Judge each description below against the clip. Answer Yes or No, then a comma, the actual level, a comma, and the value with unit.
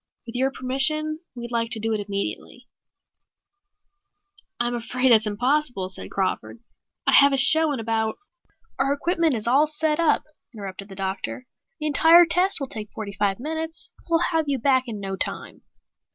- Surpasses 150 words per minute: Yes, average, 170 wpm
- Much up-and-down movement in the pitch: Yes, wide, 5.9 semitones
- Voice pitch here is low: No, very high, 255 Hz